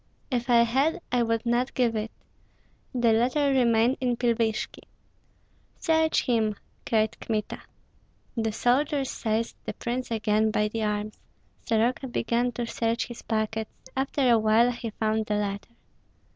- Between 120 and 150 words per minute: Yes, average, 145 wpm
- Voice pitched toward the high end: Yes, high, 230 Hz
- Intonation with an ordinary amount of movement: No, narrow, 2.1 semitones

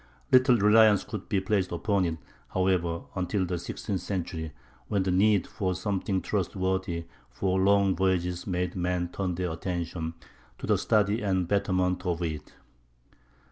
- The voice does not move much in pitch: Yes, narrow, 2.1 semitones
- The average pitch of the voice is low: Yes, very low, 95 Hz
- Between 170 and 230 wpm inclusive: No, average, 145 wpm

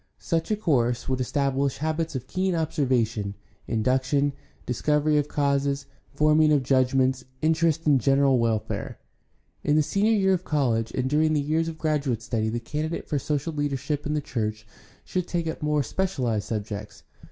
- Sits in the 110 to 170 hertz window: Yes, medium, 140 Hz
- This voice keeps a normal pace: Yes, average, 165 wpm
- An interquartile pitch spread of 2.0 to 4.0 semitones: Yes, average, 3.6 semitones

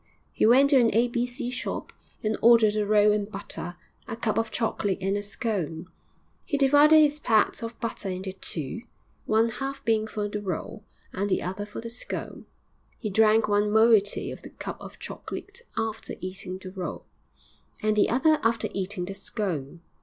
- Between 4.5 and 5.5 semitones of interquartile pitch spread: No, average, 2.8 semitones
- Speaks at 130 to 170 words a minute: No, average, 185 wpm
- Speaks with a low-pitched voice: No, high, 215 Hz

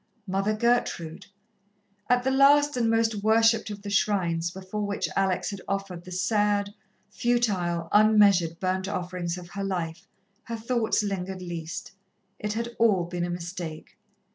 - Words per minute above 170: No, average, 145 wpm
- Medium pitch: No, high, 195 Hz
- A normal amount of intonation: Yes, average, 3.8 semitones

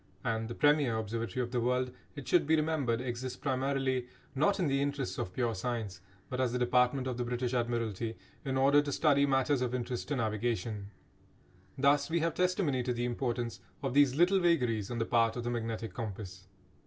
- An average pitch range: Yes, average, 3.2 semitones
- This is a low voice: Yes, low, 125 Hz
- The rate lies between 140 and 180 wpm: No, average, 195 wpm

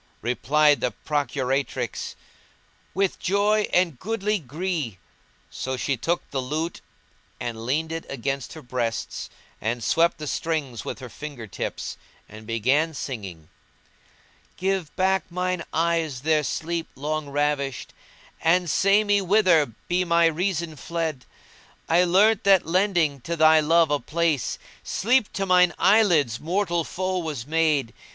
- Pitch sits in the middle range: Yes, medium, 160 Hz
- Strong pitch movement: No, average, 4.7 semitones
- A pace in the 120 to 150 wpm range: Yes, average, 140 wpm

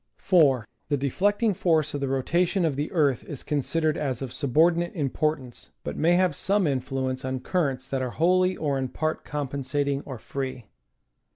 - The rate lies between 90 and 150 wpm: No, average, 175 wpm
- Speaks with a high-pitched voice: No, medium, 145 Hz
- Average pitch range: Yes, average, 4.1 semitones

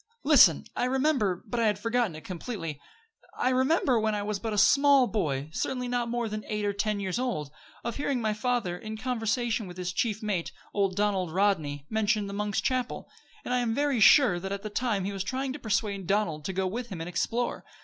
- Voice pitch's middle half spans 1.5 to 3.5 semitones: No, average, 4.2 semitones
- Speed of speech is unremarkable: No, fast, 220 wpm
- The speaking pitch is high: Yes, high, 215 Hz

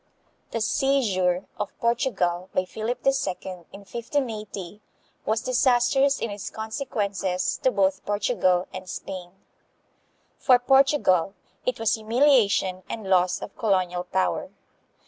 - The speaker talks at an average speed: No, slow, 115 wpm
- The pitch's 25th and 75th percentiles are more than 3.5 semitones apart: Yes, average, 4.9 semitones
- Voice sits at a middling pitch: No, high, 210 Hz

